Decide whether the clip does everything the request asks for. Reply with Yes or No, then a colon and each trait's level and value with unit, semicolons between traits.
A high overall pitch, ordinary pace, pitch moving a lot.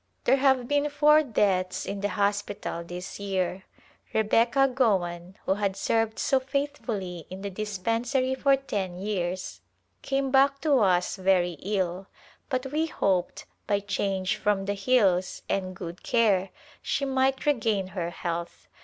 Yes: high, 205 Hz; average, 145 wpm; wide, 5.9 semitones